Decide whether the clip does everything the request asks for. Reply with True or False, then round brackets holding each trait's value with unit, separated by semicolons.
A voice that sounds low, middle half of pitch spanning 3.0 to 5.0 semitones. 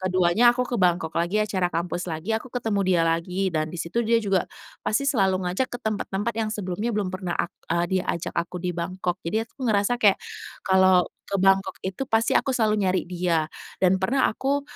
False (190 Hz; 3.5 semitones)